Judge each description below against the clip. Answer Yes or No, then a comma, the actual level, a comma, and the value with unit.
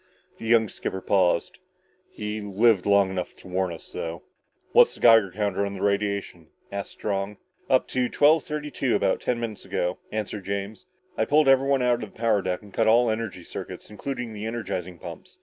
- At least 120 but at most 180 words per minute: No, average, 190 wpm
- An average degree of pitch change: Yes, average, 3.3 semitones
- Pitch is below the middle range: Yes, low, 105 Hz